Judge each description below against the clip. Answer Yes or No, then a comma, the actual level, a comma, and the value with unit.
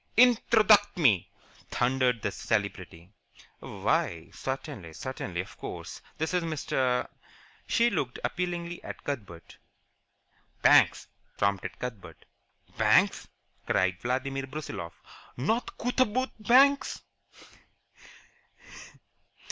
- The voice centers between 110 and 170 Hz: Yes, low, 135 Hz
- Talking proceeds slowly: Yes, slow, 90 wpm